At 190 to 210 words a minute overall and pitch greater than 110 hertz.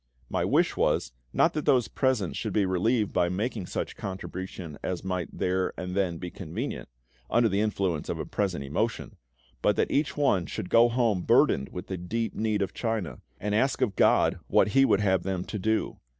No: average, 195 wpm; low, 100 Hz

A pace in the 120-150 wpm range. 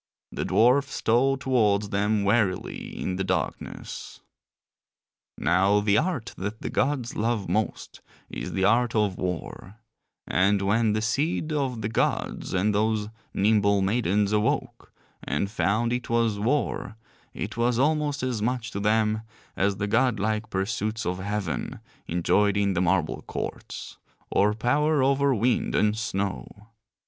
Yes: average, 140 wpm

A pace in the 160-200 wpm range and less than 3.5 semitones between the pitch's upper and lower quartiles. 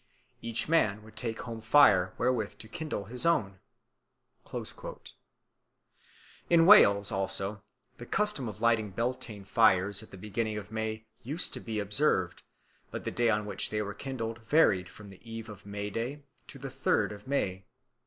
Yes: average, 165 wpm; average, 3.1 semitones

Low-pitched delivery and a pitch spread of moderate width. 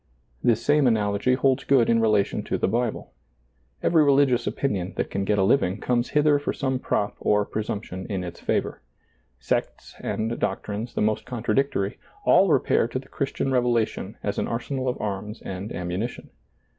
Yes: low, 115 Hz; average, 4.3 semitones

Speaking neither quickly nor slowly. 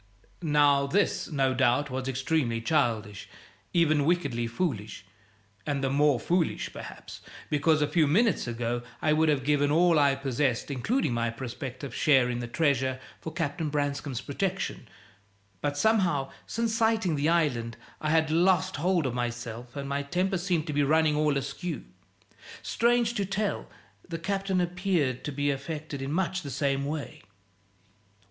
Yes: average, 155 wpm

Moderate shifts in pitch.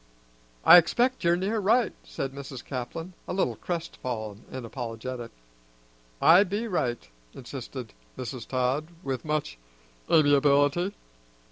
No: wide, 5.8 semitones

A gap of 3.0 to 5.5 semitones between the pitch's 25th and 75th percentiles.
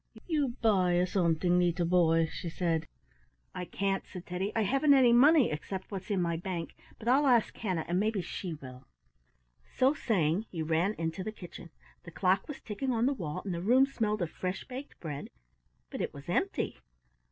Yes: average, 5.1 semitones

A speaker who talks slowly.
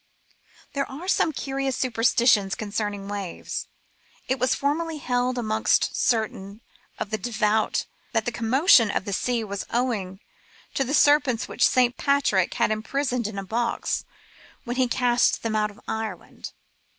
No: average, 150 wpm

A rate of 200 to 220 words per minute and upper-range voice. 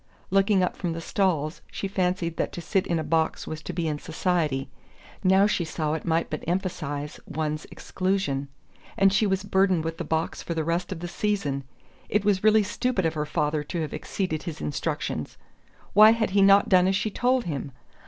No: fast, 205 wpm; medium, 175 Hz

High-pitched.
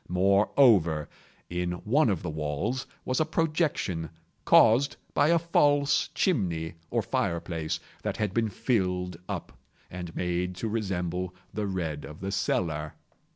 No: very low, 90 Hz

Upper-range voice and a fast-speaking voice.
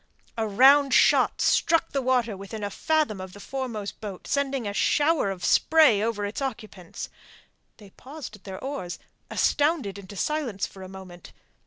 No: high, 220 Hz; average, 165 wpm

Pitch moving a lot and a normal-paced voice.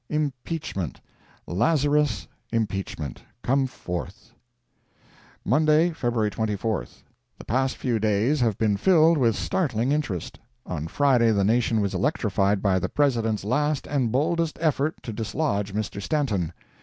No: wide, 6.2 semitones; slow, 125 wpm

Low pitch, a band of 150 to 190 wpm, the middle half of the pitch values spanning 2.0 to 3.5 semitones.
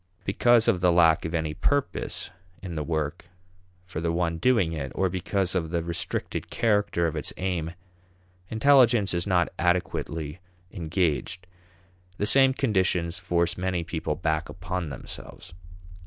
No: very low, 90 Hz; average, 140 wpm; average, 2.7 semitones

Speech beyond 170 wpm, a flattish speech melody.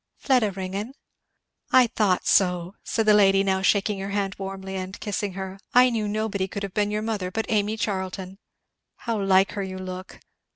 Yes: average, 180 wpm; narrow, 2.0 semitones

